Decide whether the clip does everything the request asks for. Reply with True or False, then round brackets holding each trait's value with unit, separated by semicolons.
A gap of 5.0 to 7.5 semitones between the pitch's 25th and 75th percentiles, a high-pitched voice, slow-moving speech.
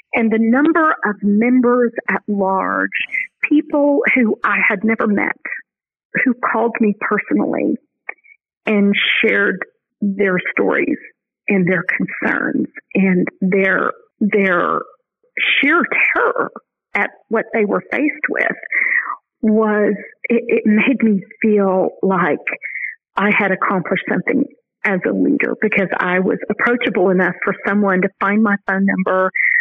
True (5.6 semitones; 215 Hz; 125 wpm)